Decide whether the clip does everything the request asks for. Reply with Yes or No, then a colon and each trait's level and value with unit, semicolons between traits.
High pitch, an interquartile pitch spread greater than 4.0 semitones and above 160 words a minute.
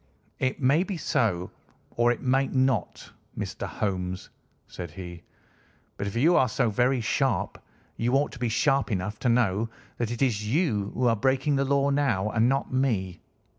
No: low, 120 Hz; average, 4.7 semitones; average, 175 wpm